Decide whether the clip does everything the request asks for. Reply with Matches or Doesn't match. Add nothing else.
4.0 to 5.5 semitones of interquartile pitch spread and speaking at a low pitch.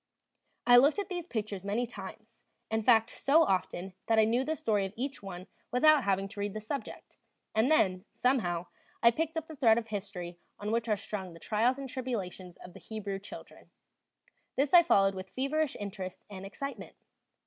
Doesn't match